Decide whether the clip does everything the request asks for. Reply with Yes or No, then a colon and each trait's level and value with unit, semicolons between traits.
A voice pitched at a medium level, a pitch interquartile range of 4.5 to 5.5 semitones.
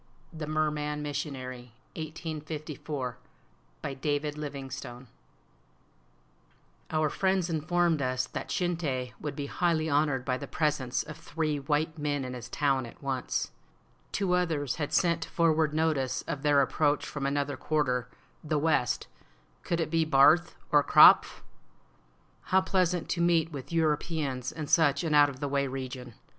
No: medium, 150 Hz; average, 2.9 semitones